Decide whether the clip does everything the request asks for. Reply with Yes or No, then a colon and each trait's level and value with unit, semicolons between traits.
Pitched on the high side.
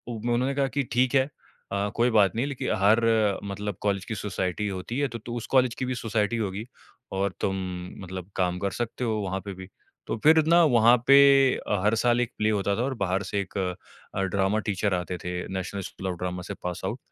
No: low, 105 Hz